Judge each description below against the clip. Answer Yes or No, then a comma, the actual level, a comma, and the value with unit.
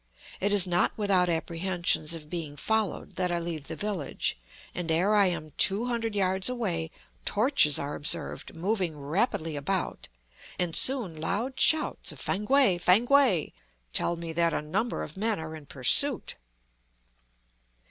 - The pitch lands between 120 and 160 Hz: No, medium, 180 Hz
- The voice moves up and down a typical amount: Yes, average, 4.6 semitones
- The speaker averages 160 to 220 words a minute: No, average, 145 wpm